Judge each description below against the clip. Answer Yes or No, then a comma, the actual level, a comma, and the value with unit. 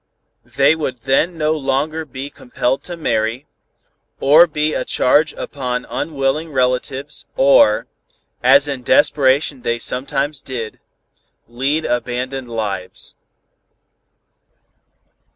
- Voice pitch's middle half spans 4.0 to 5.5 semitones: No, average, 3.0 semitones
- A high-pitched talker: No, low, 135 Hz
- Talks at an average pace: No, slow, 100 wpm